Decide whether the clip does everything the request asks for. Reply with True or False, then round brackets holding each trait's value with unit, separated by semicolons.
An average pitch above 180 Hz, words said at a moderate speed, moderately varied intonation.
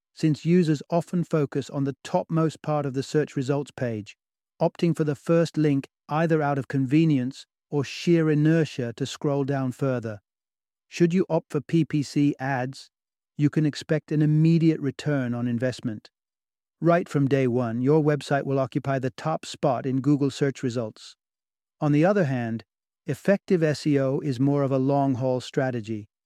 False (140 Hz; 160 wpm; 3.1 semitones)